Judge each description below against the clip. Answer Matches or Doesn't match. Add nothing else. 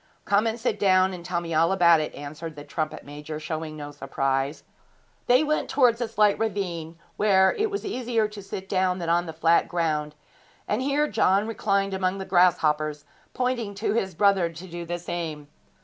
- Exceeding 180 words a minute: Matches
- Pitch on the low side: Doesn't match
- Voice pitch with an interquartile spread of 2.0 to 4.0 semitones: Doesn't match